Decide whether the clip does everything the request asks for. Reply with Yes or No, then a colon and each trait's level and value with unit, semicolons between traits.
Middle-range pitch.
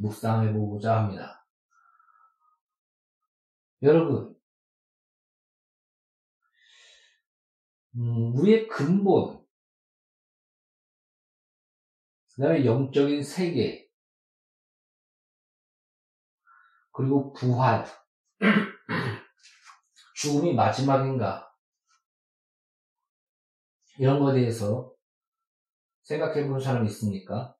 Yes: medium, 145 Hz